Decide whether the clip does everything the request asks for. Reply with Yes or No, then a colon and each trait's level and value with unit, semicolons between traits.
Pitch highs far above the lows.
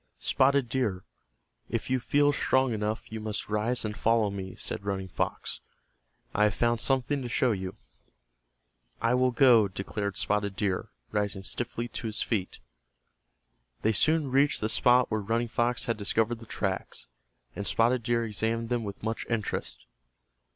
No: average, 2.9 semitones